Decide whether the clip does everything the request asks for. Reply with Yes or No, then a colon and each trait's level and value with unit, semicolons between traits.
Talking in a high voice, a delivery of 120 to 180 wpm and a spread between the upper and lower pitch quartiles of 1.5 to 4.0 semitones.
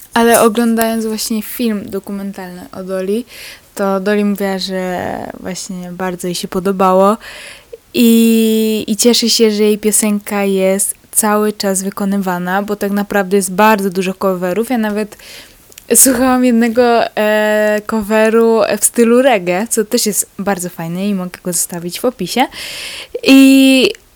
Yes: high, 210 Hz; average, 135 wpm; average, 2.8 semitones